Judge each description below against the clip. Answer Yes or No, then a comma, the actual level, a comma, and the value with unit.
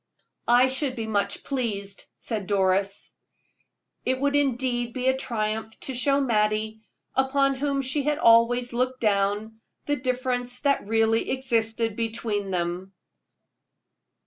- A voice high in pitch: Yes, high, 235 Hz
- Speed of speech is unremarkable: No, slow, 125 wpm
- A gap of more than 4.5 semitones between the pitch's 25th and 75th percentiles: No, average, 3.5 semitones